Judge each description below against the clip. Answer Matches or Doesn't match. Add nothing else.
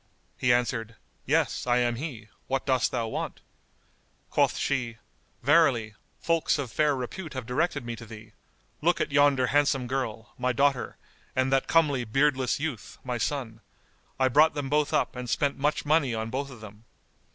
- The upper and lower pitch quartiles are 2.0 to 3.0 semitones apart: Doesn't match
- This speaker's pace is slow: Doesn't match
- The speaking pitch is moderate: Doesn't match